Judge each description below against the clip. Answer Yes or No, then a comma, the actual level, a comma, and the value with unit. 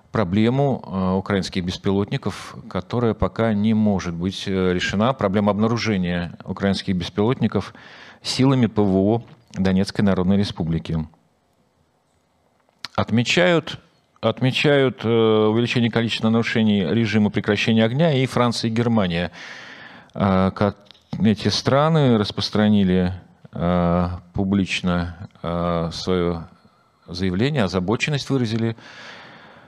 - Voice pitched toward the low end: Yes, low, 105 Hz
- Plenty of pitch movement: No, average, 3.5 semitones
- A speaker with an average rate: No, slow, 80 wpm